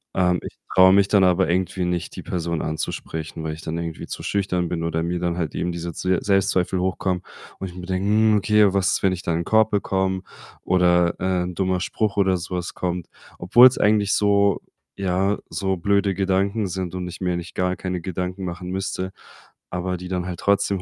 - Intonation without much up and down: Yes, narrow, 1.8 semitones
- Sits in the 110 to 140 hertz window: No, very low, 90 Hz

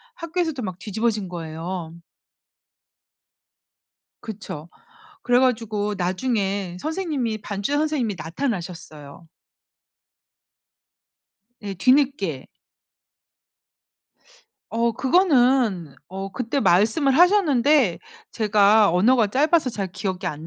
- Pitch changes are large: Yes, wide, 6.3 semitones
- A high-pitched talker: Yes, high, 215 Hz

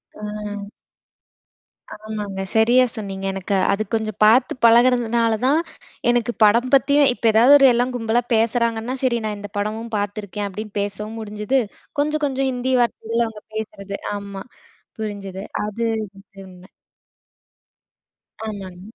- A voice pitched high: Yes, high, 220 Hz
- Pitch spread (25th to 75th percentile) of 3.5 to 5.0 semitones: No, average, 2.7 semitones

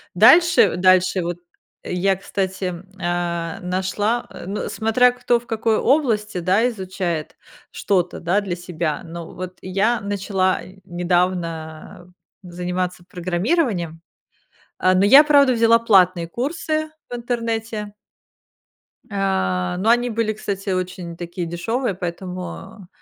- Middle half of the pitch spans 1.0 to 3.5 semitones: No, average, 4.2 semitones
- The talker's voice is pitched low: No, high, 190 Hz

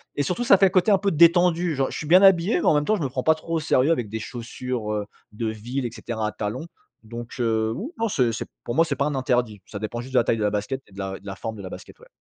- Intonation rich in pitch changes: Yes, wide, 7.0 semitones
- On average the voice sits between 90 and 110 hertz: No, low, 125 Hz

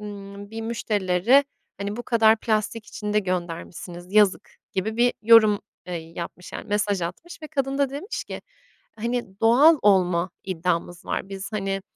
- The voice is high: Yes, high, 210 Hz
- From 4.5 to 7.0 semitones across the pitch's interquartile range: No, average, 3.6 semitones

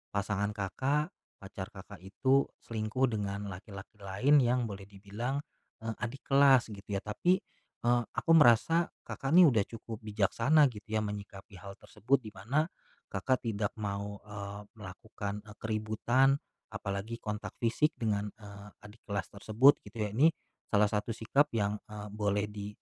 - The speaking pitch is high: No, low, 105 Hz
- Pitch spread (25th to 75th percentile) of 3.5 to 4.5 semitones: No, average, 3.0 semitones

